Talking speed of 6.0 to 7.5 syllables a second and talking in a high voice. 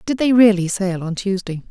No: 5.1 syllables/s; high, 200 Hz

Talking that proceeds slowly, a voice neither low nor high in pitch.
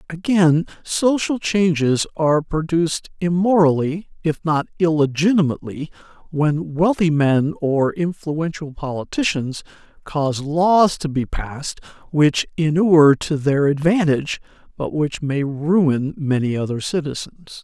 Yes: slow, 110 wpm; medium, 155 Hz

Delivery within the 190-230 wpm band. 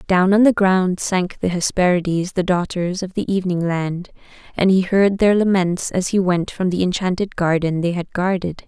Yes: average, 195 wpm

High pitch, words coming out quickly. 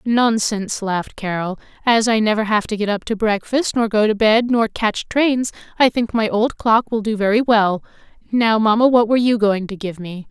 Yes: high, 220 Hz; fast, 215 wpm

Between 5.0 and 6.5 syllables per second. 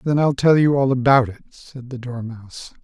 Yes: 5.7 syllables/s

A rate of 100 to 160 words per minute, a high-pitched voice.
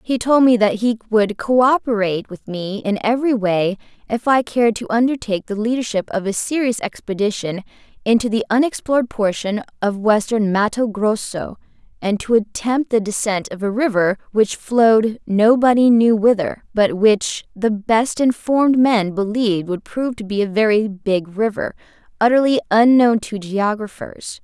Yes: average, 155 wpm; high, 220 Hz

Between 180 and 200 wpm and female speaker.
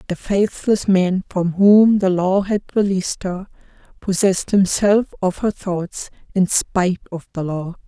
No: average, 150 wpm; female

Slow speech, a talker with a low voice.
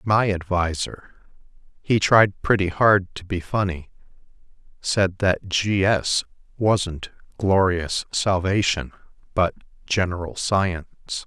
Yes: slow, 90 wpm; very low, 95 Hz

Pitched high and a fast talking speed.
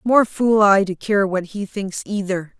Yes: high, 200 Hz; fast, 210 wpm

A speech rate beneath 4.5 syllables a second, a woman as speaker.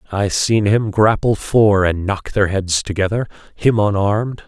No: 4.3 syllables/s; male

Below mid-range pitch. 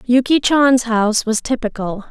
No: high, 240 Hz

